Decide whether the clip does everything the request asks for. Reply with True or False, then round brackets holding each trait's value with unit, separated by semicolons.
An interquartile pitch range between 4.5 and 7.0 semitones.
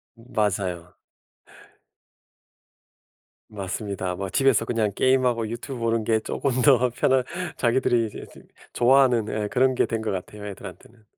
False (3.4 semitones)